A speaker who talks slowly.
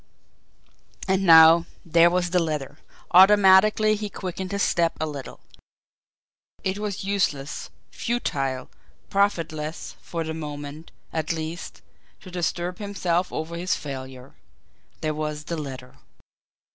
Yes: slow, 120 wpm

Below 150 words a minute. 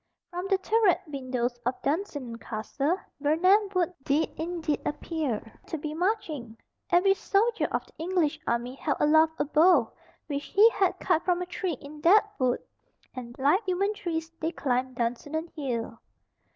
No: average, 155 wpm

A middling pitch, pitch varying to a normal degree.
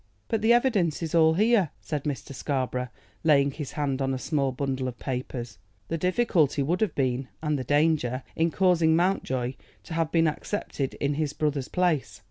Yes: medium, 150 Hz; average, 3.9 semitones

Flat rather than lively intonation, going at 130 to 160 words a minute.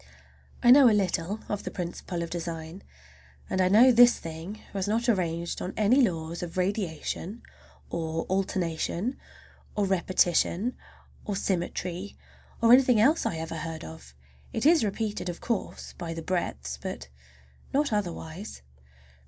No: average, 4.6 semitones; average, 145 wpm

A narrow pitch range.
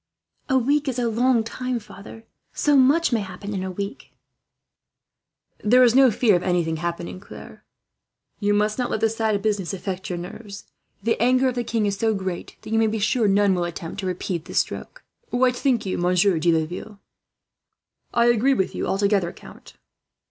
No: average, 4.3 semitones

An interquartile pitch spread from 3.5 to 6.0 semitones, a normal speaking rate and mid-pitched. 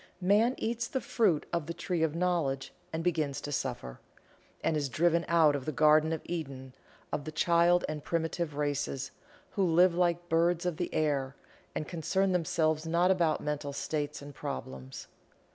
No: average, 3.1 semitones; average, 175 wpm; medium, 160 Hz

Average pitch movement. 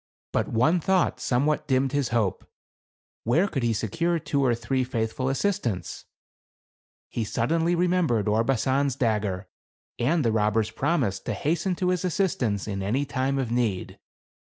No: wide, 6.4 semitones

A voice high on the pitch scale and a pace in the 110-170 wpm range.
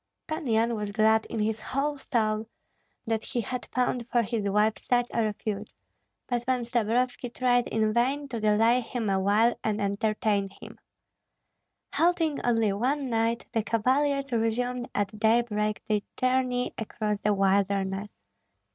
Yes: high, 225 Hz; average, 145 wpm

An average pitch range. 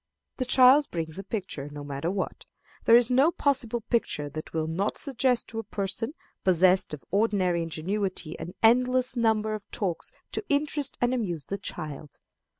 No: wide, 6.5 semitones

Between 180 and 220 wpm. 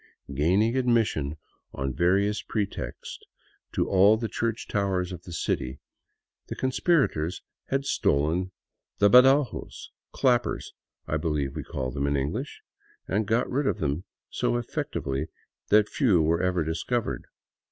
No: average, 145 wpm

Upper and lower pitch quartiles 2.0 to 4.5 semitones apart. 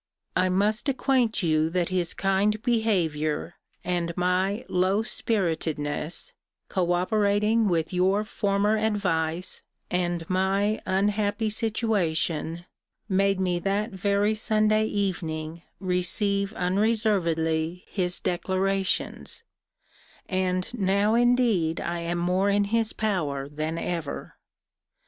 Yes: average, 3.4 semitones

